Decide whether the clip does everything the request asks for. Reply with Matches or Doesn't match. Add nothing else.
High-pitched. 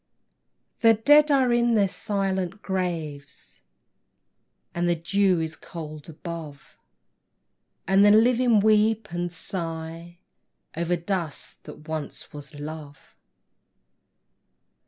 Doesn't match